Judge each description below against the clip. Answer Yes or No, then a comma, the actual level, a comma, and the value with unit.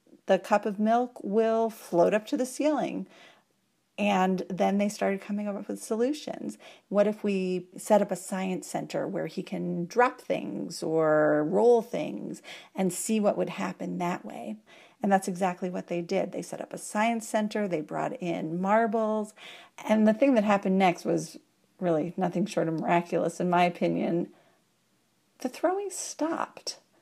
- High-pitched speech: Yes, high, 200 Hz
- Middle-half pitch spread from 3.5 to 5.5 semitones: Yes, average, 3.9 semitones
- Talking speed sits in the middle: Yes, average, 165 wpm